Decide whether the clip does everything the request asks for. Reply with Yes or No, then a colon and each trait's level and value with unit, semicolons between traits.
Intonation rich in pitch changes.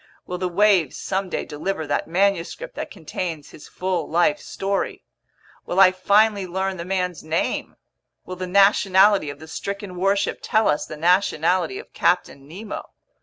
No: average, 2.8 semitones